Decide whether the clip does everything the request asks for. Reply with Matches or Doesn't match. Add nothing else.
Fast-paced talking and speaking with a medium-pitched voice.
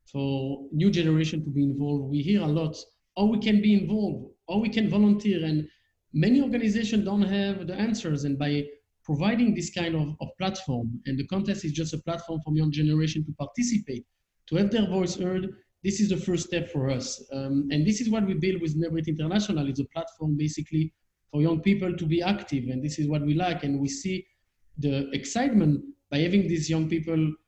Matches